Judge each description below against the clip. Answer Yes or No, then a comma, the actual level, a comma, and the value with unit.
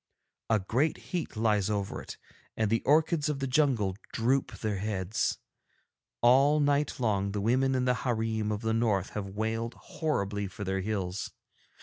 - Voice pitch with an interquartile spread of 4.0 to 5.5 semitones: Yes, average, 4.4 semitones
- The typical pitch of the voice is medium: No, low, 110 Hz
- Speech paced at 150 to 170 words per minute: Yes, average, 160 wpm